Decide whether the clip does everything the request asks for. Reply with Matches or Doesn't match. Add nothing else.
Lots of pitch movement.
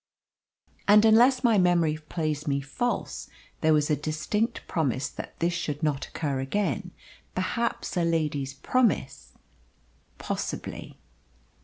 Matches